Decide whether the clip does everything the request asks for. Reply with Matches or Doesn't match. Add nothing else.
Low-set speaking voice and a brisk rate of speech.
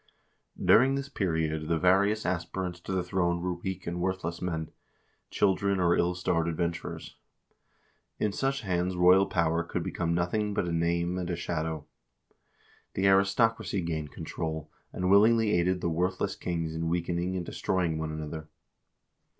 Doesn't match